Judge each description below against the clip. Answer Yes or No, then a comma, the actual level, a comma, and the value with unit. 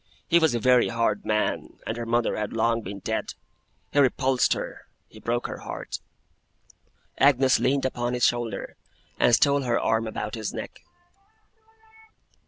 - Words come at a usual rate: Yes, average, 155 wpm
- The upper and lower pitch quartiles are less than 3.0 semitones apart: Yes, narrow, 2.4 semitones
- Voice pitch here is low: Yes, low, 120 Hz